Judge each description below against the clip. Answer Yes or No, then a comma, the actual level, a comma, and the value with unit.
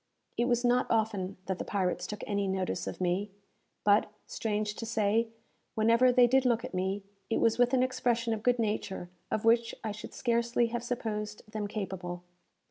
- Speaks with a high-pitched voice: Yes, high, 220 Hz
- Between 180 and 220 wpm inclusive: Yes, average, 185 wpm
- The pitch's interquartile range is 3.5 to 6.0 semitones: No, average, 2.8 semitones